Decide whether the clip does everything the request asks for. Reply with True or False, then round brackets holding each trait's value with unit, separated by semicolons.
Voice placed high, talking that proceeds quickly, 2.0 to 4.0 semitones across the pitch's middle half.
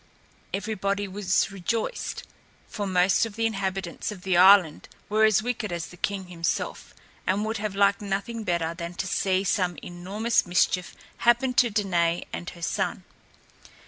False (195 Hz; 155 wpm; 3.1 semitones)